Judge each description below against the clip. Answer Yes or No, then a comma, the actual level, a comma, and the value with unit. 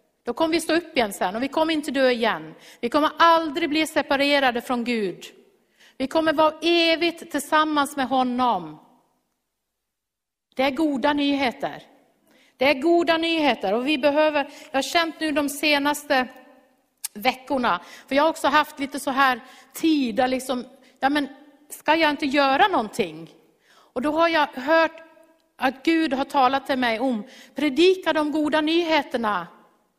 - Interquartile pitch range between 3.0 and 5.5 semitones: Yes, average, 3.3 semitones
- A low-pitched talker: No, very high, 280 Hz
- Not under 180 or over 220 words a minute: No, average, 155 wpm